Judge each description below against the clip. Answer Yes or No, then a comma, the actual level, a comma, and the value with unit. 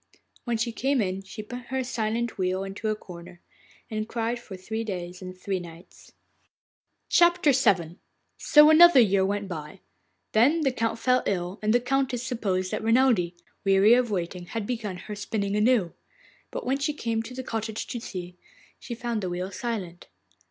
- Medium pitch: No, high, 215 Hz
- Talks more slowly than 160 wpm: No, average, 175 wpm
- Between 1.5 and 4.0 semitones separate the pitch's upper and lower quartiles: No, average, 4.6 semitones